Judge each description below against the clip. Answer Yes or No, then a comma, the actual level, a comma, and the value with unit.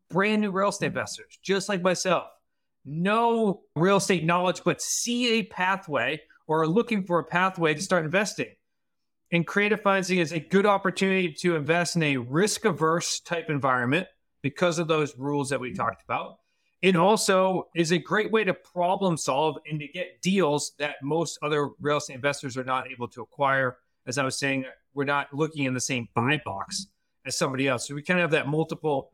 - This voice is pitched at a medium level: Yes, medium, 170 Hz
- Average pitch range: Yes, average, 4.9 semitones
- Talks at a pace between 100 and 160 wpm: No, average, 195 wpm